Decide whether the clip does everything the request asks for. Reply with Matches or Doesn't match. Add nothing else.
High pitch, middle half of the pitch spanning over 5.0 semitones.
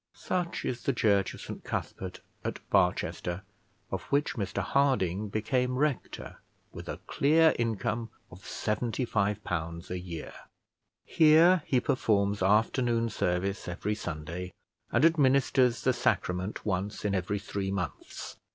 Doesn't match